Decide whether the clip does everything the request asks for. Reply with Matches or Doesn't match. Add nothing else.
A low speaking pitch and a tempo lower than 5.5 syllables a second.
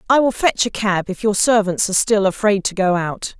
Doesn't match